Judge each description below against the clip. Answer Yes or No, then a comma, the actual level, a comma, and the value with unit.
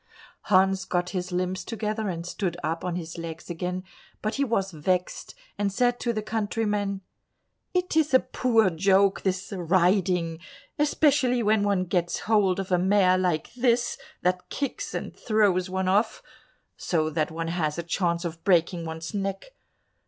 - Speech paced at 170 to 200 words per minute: No, average, 160 wpm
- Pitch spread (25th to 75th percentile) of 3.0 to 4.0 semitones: Yes, average, 3.5 semitones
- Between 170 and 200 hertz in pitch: Yes, high, 190 Hz